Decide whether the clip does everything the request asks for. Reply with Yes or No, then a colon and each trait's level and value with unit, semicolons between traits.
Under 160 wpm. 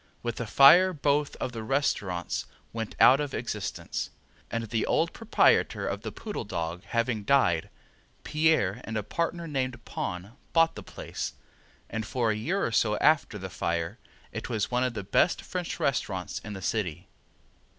No: average, 170 wpm